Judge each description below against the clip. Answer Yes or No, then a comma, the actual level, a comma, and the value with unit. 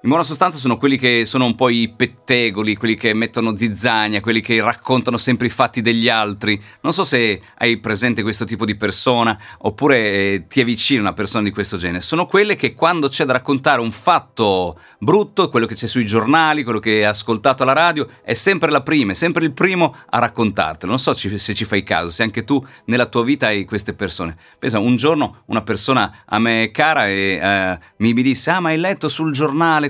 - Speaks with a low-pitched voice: Yes, low, 115 Hz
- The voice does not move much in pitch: No, average, 4.5 semitones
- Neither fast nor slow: No, fast, 210 wpm